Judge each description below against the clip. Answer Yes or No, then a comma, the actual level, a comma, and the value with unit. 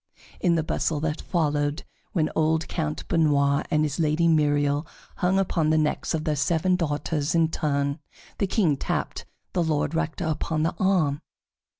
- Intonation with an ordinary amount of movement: No, narrow, 2.1 semitones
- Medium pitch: Yes, medium, 155 Hz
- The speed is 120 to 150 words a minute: No, average, 165 wpm